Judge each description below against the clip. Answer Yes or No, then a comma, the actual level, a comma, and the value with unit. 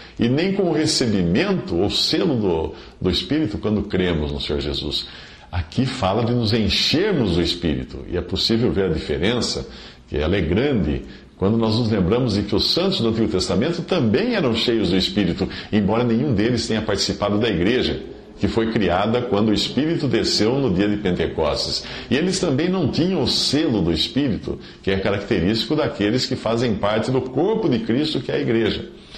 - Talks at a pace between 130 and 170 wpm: No, fast, 185 wpm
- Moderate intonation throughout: Yes, average, 4.3 semitones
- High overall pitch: No, low, 105 Hz